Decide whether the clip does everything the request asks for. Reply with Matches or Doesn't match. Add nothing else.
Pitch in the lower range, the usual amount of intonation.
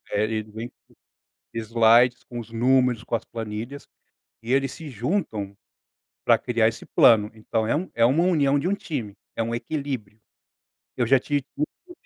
Matches